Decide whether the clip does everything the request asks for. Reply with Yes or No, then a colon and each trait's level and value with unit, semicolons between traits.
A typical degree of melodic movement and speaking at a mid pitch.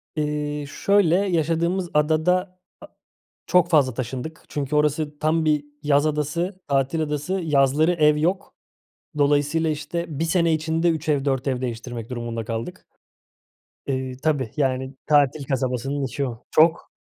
Yes: average, 3.1 semitones; medium, 150 Hz